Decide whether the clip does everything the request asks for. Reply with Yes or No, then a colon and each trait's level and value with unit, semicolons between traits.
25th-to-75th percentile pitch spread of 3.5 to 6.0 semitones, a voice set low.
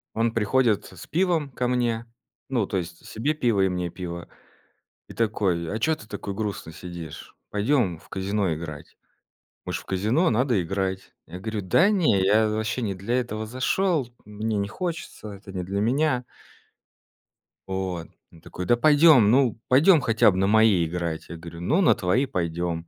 Yes: average, 5.3 semitones; low, 105 Hz